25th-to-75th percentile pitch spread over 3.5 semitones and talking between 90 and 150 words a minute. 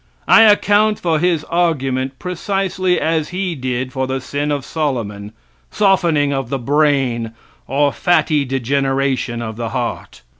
Yes: average, 4.8 semitones; average, 140 wpm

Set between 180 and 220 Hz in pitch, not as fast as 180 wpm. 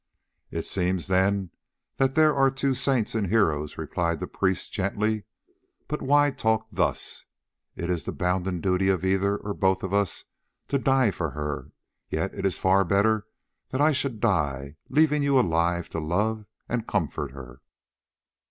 No: low, 100 Hz; average, 160 wpm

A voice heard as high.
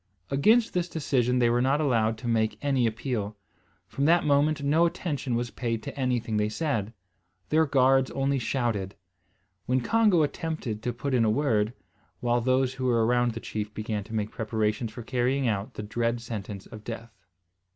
No: low, 120 Hz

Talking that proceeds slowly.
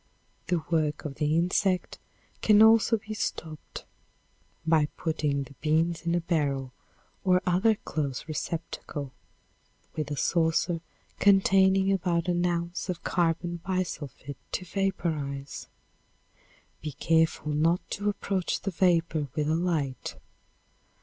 Yes: slow, 125 wpm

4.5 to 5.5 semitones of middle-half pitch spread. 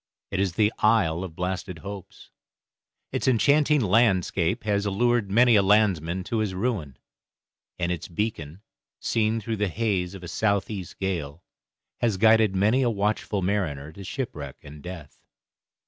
No: average, 3.7 semitones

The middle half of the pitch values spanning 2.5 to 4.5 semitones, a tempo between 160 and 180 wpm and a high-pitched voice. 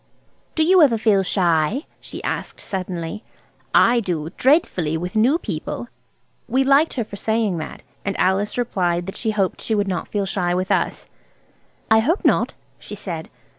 No: average, 4.9 semitones; average, 170 wpm; high, 200 Hz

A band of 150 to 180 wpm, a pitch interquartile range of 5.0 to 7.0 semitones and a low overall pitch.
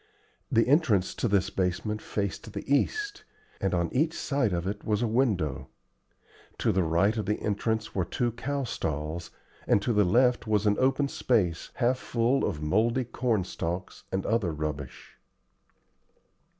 Yes: average, 160 wpm; average, 5.3 semitones; low, 105 Hz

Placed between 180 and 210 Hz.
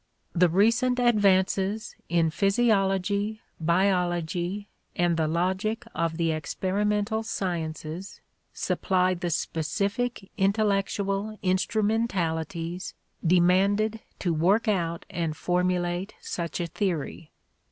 Yes: medium, 185 Hz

